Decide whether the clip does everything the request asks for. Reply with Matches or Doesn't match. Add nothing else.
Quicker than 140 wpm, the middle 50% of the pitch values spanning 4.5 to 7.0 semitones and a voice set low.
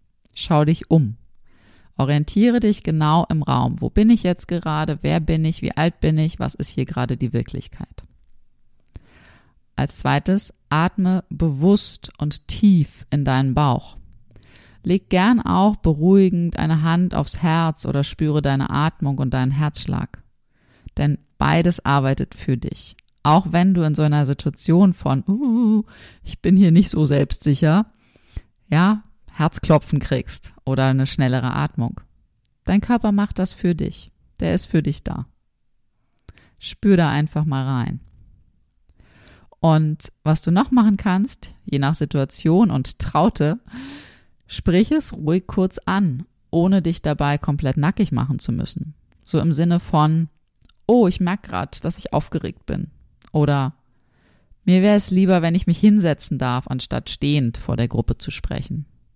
Doesn't match